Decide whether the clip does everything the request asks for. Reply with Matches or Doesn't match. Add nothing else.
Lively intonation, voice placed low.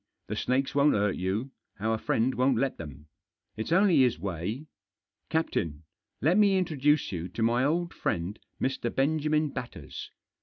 Matches